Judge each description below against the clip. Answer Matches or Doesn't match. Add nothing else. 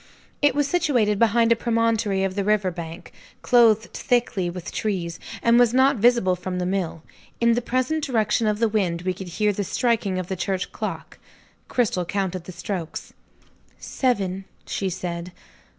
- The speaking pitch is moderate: Doesn't match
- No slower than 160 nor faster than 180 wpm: Matches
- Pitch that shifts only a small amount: Doesn't match